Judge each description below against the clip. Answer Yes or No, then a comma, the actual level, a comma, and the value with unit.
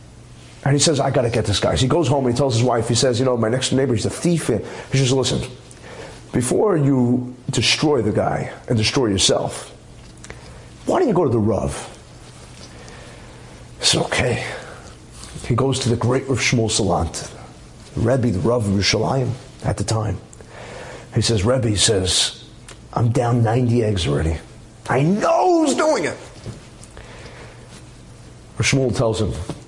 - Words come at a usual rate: Yes, average, 170 wpm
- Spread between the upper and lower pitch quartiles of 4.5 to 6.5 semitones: No, average, 3.1 semitones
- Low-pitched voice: Yes, low, 120 Hz